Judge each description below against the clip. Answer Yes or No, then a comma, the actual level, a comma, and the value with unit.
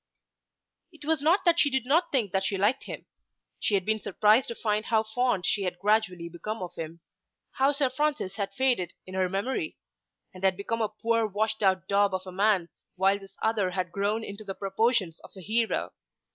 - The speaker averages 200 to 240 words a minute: Yes, fast, 205 wpm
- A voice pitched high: Yes, high, 210 Hz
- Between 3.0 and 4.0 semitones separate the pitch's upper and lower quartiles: Yes, average, 3.6 semitones